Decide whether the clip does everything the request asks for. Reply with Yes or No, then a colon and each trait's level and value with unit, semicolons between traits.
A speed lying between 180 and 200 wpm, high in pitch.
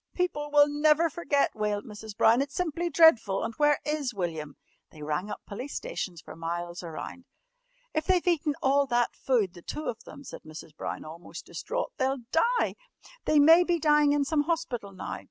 Yes: average, 185 wpm; very high, 275 Hz